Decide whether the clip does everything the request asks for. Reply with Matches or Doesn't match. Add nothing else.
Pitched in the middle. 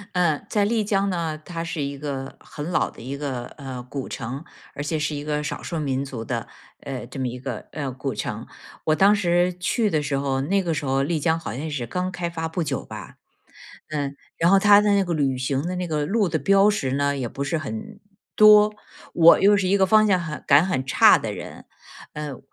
Matches